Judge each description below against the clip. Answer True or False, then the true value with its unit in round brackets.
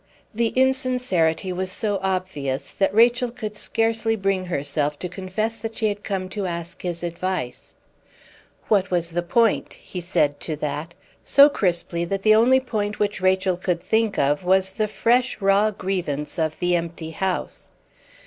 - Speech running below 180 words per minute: True (160 wpm)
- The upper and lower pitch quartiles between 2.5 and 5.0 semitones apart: True (4.1 semitones)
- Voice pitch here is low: False (190 Hz)